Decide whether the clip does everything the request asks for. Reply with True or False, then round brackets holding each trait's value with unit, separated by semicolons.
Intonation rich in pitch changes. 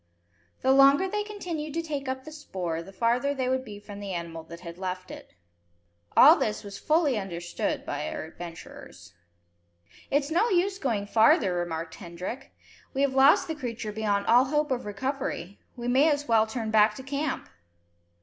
True (6.6 semitones)